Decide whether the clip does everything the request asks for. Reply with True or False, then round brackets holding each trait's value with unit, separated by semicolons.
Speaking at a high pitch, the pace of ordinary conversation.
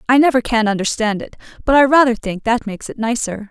False (230 Hz; 225 wpm)